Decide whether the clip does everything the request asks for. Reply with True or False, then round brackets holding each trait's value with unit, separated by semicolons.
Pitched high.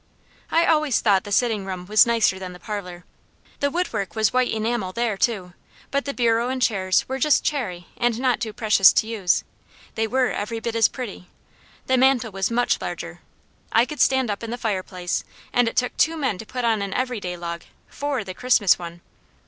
True (225 Hz)